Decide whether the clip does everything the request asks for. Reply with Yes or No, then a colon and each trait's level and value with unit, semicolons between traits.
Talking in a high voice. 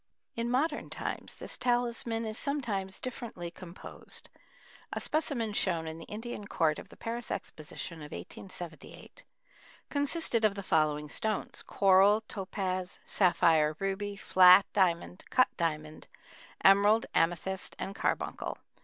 Yes: high, 195 Hz